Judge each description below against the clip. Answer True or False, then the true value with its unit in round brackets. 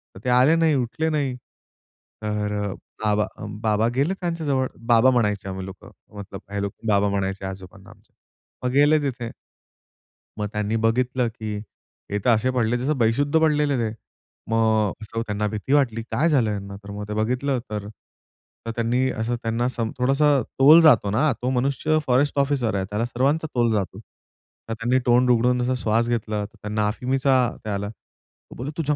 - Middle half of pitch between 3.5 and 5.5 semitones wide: True (4.1 semitones)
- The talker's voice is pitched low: True (120 Hz)